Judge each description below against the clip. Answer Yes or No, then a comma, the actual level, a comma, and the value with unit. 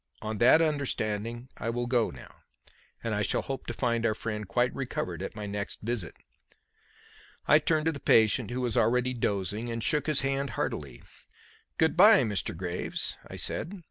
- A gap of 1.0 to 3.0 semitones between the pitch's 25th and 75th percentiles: No, average, 4.4 semitones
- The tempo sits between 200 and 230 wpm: No, average, 175 wpm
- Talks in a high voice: No, low, 120 Hz